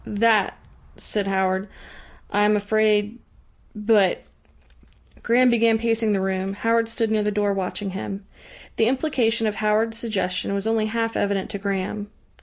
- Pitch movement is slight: Yes, narrow, 2.3 semitones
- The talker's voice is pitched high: Yes, high, 210 Hz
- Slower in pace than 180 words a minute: Yes, average, 150 wpm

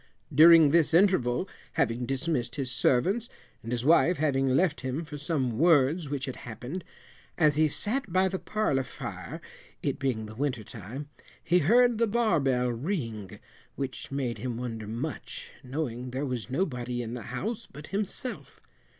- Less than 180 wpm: Yes, average, 160 wpm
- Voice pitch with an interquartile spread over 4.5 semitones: Yes, average, 5.3 semitones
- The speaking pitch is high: No, low, 135 Hz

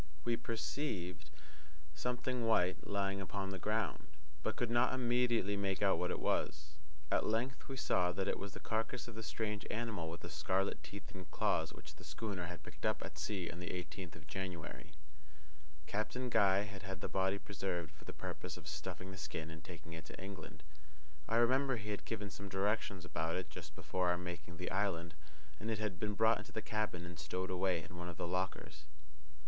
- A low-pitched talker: Yes, very low, 95 Hz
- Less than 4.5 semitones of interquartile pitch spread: Yes, average, 3.8 semitones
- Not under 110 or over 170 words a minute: No, average, 200 wpm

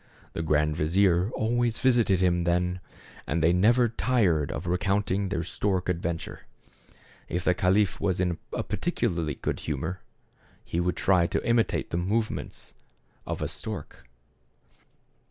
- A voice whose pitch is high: No, very low, 90 Hz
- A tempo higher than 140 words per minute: No, slow, 135 wpm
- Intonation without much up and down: No, average, 3.3 semitones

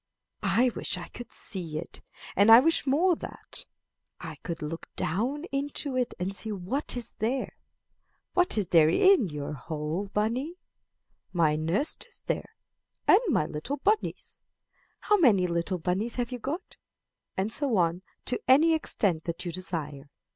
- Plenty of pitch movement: Yes, wide, 8.1 semitones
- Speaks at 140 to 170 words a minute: Yes, average, 155 wpm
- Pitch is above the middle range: Yes, high, 210 Hz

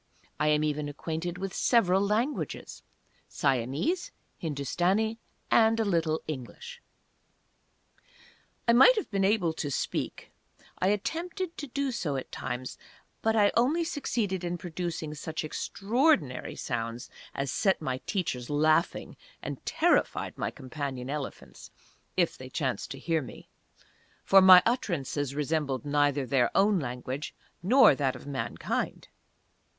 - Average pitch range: No, wide, 7.2 semitones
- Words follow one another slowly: Yes, slow, 130 wpm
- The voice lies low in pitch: No, medium, 165 Hz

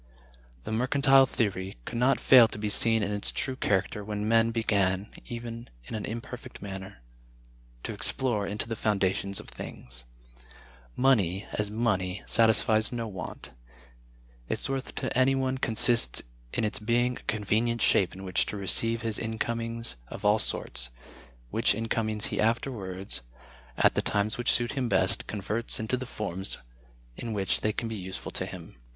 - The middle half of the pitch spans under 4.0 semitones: Yes, average, 2.9 semitones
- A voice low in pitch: Yes, low, 110 Hz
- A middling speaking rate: Yes, average, 160 wpm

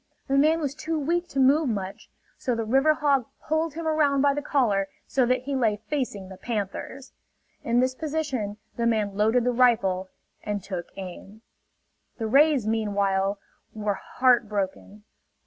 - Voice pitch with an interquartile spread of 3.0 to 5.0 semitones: No, wide, 5.5 semitones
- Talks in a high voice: Yes, high, 240 Hz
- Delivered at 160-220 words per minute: Yes, average, 165 wpm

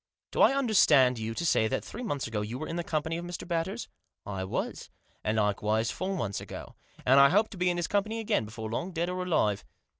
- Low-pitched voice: No, medium, 160 Hz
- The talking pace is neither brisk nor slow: No, fast, 245 wpm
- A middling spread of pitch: No, wide, 8.6 semitones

